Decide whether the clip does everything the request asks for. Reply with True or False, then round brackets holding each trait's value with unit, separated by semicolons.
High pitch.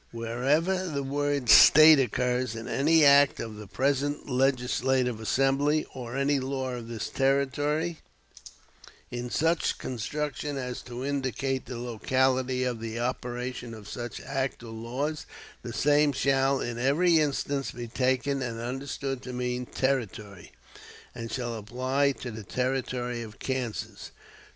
False (130 Hz)